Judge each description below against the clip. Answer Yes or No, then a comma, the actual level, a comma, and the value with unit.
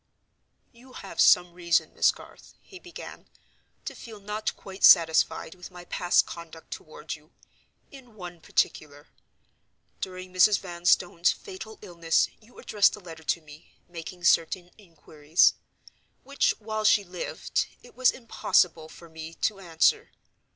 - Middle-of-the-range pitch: Yes, medium, 180 Hz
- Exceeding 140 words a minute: No, slow, 135 wpm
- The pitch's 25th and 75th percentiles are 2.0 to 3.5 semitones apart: No, average, 4.2 semitones